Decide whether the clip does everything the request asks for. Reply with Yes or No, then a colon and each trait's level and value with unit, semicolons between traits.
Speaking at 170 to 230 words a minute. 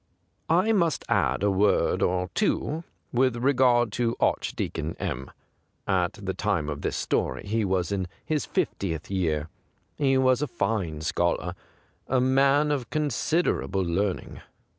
No: average, 140 wpm